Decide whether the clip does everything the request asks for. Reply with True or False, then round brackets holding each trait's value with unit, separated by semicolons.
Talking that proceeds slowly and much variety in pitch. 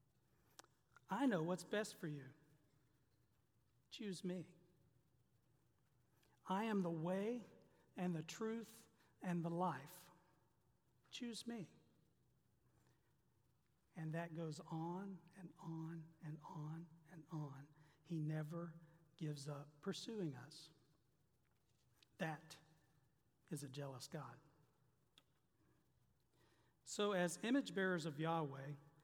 False (95 wpm; 3.9 semitones)